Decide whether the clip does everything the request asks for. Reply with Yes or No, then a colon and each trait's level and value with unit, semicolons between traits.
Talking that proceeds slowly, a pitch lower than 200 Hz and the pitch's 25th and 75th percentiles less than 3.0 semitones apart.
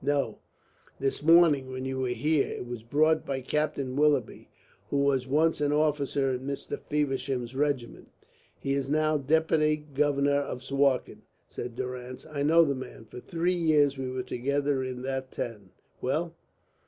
No: average, 165 wpm; medium, 140 Hz; narrow, 2.5 semitones